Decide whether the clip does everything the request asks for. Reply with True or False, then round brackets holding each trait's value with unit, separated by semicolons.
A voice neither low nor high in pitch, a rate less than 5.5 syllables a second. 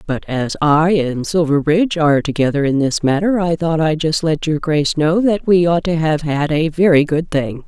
True (160 Hz; 5.0 syllables/s)